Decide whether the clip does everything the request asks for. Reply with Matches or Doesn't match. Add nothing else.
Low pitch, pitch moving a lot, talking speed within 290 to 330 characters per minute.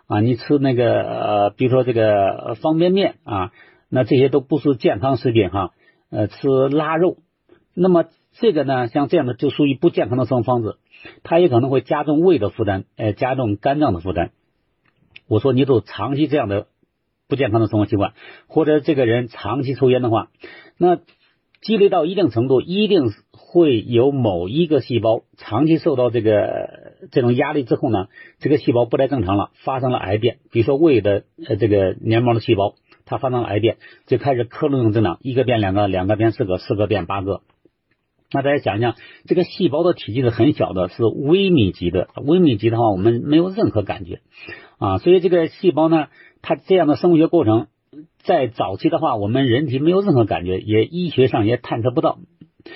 Matches